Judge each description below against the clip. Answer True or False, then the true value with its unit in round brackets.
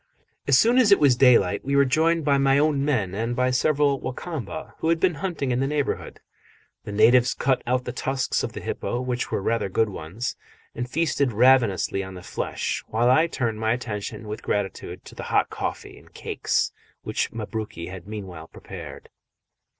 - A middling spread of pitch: True (4.6 semitones)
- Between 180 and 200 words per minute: True (190 wpm)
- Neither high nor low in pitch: False (125 Hz)